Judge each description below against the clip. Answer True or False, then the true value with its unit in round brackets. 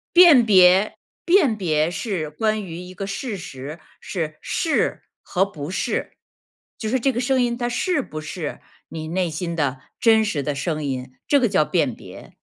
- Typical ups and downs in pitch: False (7.4 semitones)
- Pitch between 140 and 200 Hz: True (185 Hz)